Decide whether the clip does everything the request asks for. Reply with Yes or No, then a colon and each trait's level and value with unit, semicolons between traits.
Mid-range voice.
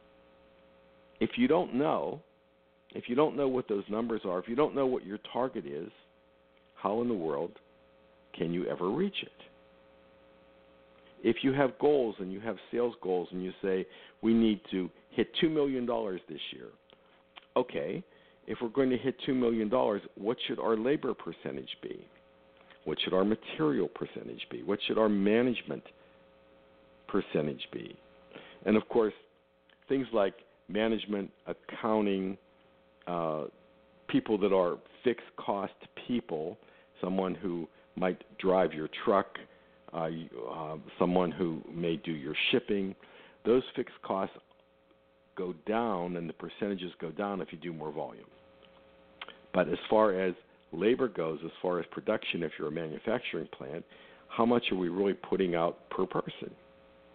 No: very low, 85 Hz